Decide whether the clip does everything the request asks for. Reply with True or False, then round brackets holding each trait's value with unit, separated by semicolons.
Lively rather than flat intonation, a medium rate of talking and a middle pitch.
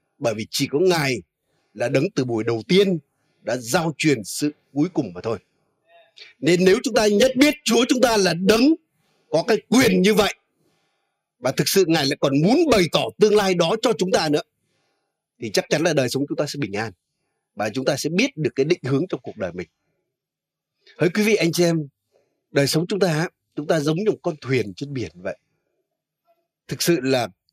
True (6.5 semitones; 215 wpm; 160 Hz)